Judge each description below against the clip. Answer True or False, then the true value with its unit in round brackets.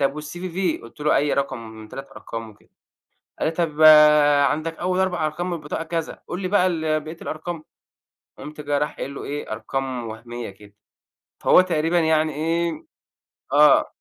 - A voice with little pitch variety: False (3.6 semitones)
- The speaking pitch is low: False (155 Hz)